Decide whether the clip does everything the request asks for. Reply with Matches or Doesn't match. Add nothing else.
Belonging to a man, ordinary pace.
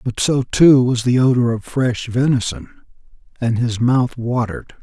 Matches